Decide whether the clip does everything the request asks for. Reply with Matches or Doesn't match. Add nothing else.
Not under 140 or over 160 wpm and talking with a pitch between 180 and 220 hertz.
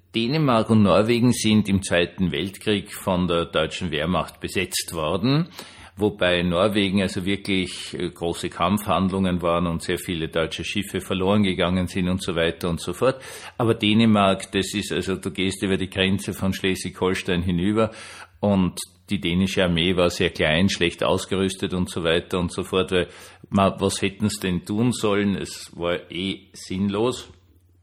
Doesn't match